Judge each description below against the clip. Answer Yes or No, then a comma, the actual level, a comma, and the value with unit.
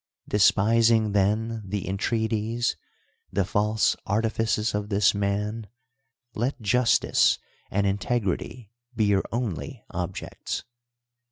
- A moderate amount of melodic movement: No, narrow, 2.2 semitones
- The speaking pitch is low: Yes, low, 105 Hz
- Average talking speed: No, slow, 105 wpm